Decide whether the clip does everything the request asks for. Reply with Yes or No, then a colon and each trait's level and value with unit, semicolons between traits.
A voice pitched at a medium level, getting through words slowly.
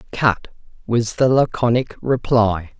No: low, 115 Hz; slow, 105 wpm